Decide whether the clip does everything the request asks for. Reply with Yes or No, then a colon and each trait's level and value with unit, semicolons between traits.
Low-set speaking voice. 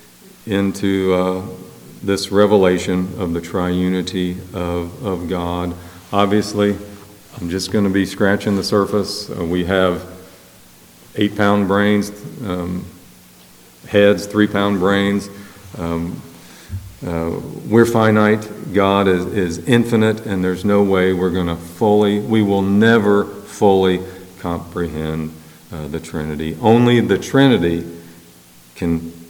Yes: very low, 95 Hz